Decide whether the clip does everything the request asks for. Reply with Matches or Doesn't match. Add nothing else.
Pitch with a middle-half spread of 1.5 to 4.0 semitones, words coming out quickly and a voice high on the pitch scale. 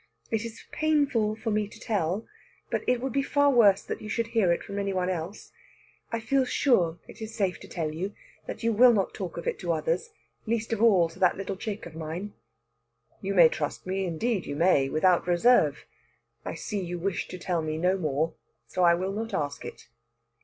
Doesn't match